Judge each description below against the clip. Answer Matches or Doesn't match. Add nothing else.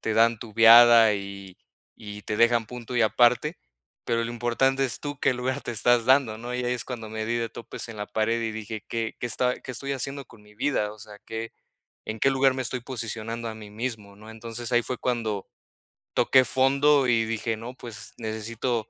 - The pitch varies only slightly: Matches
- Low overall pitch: Matches